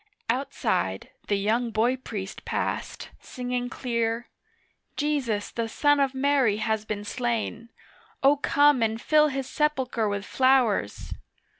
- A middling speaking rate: No, slow, 125 wpm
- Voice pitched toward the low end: No, high, 240 Hz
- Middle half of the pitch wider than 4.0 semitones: No, average, 3.7 semitones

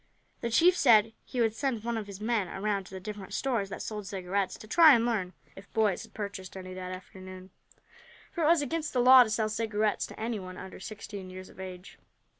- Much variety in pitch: No, average, 3.7 semitones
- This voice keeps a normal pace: No, fast, 220 wpm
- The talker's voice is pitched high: Yes, high, 210 Hz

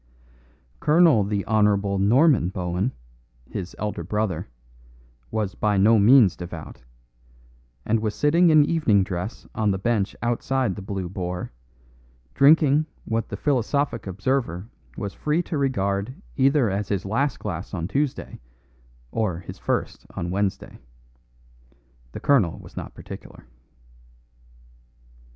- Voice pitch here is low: Yes, low, 105 Hz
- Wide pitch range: Yes, wide, 5.8 semitones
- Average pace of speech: No, slow, 125 wpm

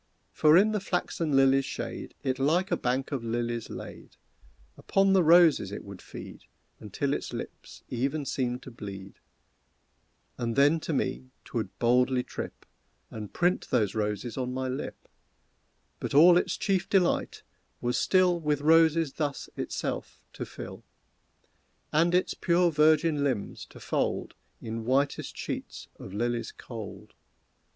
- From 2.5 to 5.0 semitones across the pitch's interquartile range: No, wide, 5.5 semitones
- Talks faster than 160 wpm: No, average, 145 wpm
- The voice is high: No, low, 135 Hz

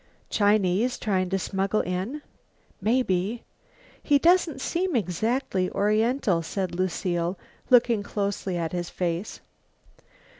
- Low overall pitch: No, high, 200 Hz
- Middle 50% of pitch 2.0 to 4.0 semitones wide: No, average, 4.7 semitones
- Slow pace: Yes, slow, 105 wpm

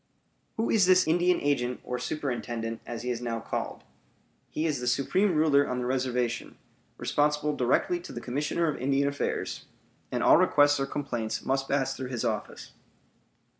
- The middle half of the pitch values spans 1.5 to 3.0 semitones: No, average, 3.6 semitones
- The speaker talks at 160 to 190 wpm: Yes, average, 170 wpm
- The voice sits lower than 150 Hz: Yes, low, 135 Hz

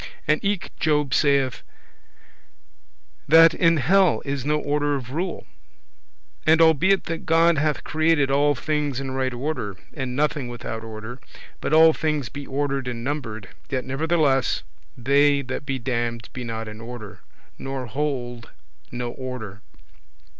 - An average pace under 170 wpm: Yes, average, 140 wpm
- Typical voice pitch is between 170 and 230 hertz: No, medium, 140 Hz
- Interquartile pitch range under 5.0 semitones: Yes, average, 3.7 semitones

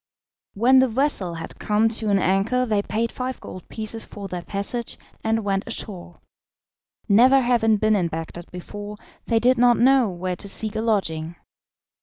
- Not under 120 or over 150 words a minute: No, average, 170 wpm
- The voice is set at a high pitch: Yes, high, 215 Hz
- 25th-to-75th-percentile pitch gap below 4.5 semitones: Yes, average, 3.5 semitones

